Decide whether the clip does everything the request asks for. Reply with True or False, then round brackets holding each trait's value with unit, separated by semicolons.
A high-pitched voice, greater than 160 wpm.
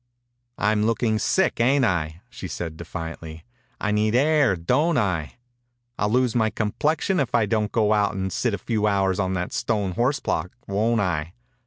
False (105 Hz; 180 wpm)